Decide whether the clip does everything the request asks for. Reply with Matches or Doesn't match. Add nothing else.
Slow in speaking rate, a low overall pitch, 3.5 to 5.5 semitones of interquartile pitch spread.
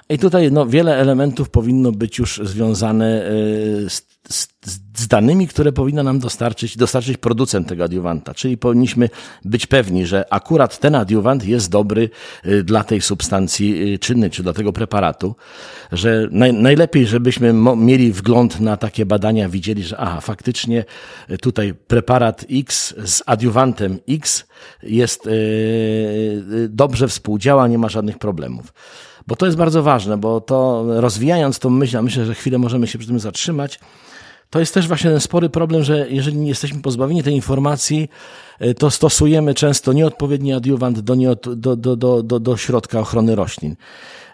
Doesn't match